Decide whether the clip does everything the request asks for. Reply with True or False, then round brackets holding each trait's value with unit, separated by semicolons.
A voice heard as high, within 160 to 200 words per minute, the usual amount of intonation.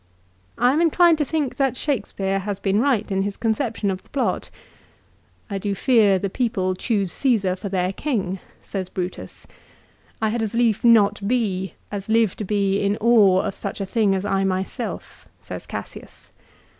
True (205 Hz; 185 wpm; 3.5 semitones)